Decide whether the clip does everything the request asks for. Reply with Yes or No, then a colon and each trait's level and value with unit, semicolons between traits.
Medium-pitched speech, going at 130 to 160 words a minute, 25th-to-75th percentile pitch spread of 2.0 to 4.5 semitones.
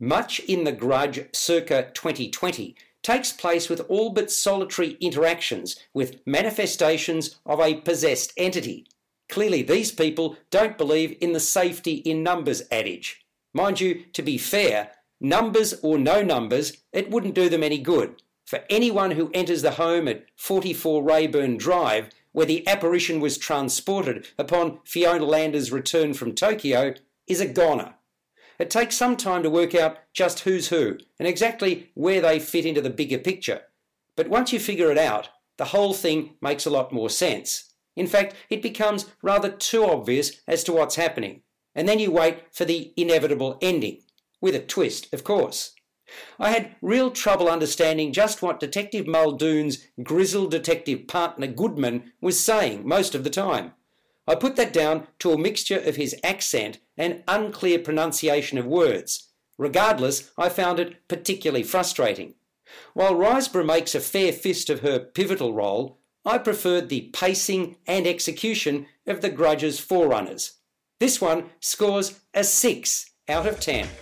Yes: medium, 170 Hz; average, 155 wpm; average, 4.0 semitones